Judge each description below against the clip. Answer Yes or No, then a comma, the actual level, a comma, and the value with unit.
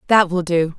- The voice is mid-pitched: Yes, medium, 180 Hz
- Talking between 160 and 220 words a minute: No, fast, 230 wpm